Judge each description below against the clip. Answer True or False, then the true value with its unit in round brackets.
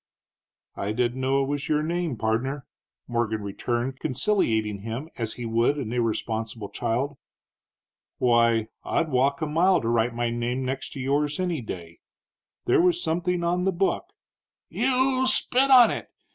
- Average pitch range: False (6.3 semitones)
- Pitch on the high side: False (130 Hz)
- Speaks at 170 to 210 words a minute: False (160 wpm)